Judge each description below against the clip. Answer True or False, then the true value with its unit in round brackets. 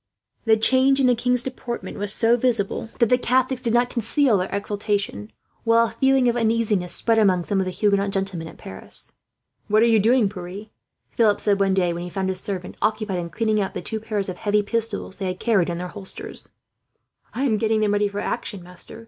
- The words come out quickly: True (215 wpm)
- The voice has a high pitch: True (210 Hz)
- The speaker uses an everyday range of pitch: True (3.3 semitones)